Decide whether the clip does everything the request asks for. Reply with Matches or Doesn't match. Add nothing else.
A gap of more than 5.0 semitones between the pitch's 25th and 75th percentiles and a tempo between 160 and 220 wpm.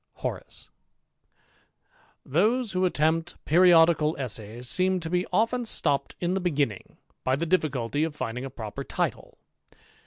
Doesn't match